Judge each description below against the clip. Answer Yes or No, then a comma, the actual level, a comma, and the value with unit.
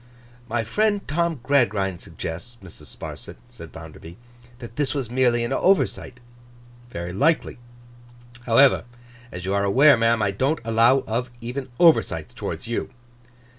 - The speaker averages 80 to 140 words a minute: Yes, slow, 135 wpm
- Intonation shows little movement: No, wide, 5.6 semitones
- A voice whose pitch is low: Yes, low, 120 Hz